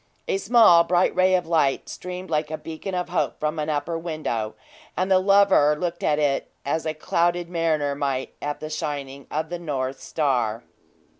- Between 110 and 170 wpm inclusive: No, average, 180 wpm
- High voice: No, medium, 155 Hz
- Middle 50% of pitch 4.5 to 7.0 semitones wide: No, average, 3.3 semitones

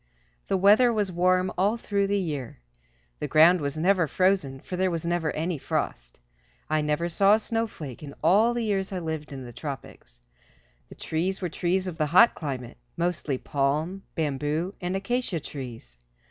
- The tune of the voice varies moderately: Yes, average, 4.6 semitones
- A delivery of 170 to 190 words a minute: Yes, average, 175 wpm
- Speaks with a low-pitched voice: No, medium, 170 Hz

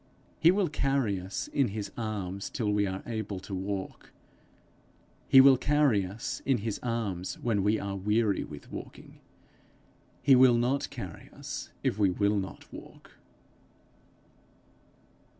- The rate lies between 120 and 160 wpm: Yes, average, 140 wpm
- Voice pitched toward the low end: Yes, low, 105 Hz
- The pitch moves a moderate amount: Yes, average, 4.2 semitones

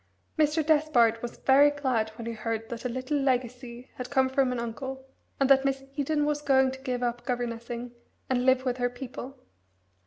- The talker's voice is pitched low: No, very high, 255 Hz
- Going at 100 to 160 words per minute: No, average, 190 wpm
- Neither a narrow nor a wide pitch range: No, narrow, 2.2 semitones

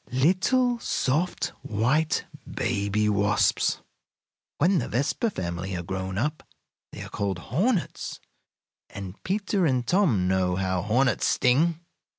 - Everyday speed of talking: No, slow, 120 wpm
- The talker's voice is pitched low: Yes, low, 125 Hz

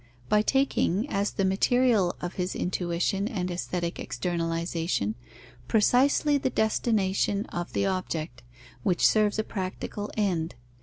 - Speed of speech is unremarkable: No, slow, 120 wpm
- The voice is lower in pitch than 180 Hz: No, high, 190 Hz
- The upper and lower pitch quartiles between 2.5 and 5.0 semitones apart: Yes, average, 3.6 semitones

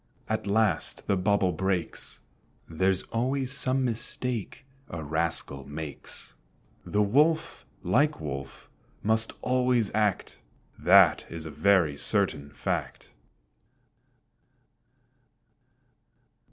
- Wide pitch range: Yes, wide, 7.2 semitones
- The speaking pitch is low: Yes, low, 100 Hz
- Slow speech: Yes, slow, 90 wpm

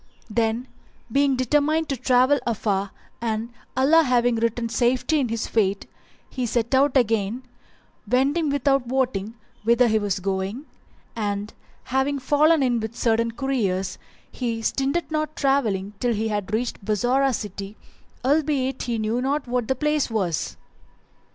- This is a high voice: Yes, high, 245 Hz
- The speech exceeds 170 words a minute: No, average, 145 wpm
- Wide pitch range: No, average, 3.8 semitones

